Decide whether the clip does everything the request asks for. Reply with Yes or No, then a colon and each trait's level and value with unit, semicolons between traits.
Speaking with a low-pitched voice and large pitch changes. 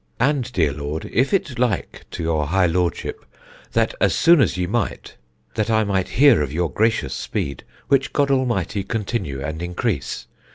Yes: low, 100 Hz; wide, 6.7 semitones